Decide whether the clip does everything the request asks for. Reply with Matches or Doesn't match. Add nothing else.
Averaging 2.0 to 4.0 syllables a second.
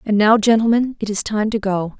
Doesn't match